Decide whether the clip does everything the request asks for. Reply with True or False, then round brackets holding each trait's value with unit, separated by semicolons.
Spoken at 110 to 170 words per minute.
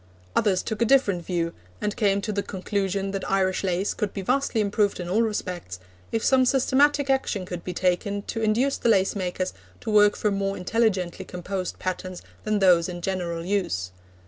False (185 wpm)